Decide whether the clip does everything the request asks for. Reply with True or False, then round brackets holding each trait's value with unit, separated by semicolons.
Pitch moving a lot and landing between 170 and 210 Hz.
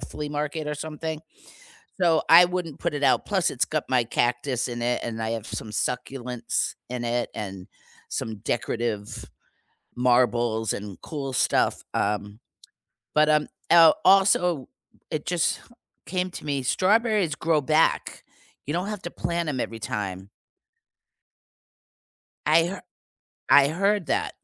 False (5.9 semitones; 145 Hz)